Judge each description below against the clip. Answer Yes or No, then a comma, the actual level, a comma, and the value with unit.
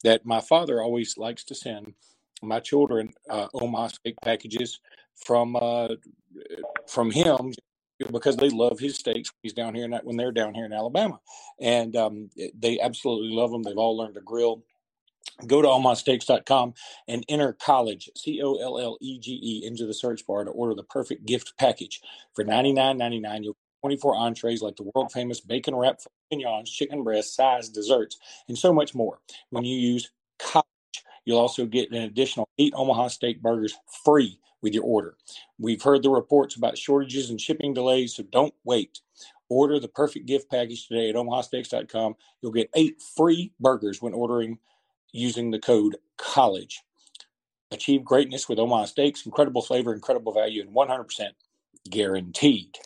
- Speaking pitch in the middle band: No, low, 120 Hz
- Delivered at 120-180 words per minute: Yes, average, 165 wpm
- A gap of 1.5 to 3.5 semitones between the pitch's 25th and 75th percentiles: Yes, average, 2.9 semitones